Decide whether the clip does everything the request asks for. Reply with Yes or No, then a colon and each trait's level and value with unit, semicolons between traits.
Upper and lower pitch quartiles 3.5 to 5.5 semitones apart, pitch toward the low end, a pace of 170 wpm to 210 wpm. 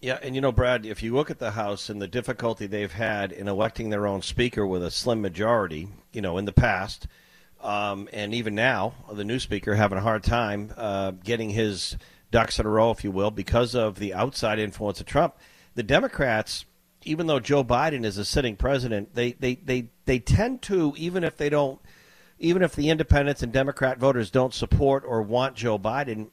Yes: average, 4.1 semitones; low, 115 Hz; fast, 205 wpm